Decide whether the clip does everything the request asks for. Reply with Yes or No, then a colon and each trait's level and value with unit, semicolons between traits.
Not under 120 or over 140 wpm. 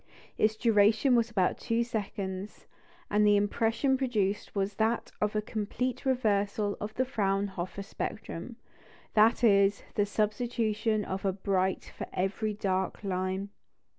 Yes: slow, 135 wpm